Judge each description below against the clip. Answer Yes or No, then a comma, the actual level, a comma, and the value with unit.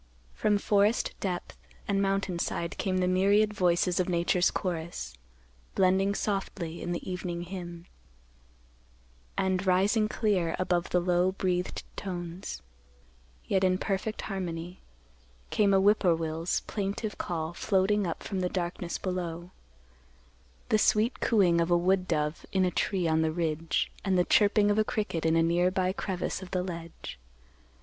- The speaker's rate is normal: Yes, average, 150 wpm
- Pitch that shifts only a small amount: Yes, narrow, 2.3 semitones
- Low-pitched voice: No, medium, 185 Hz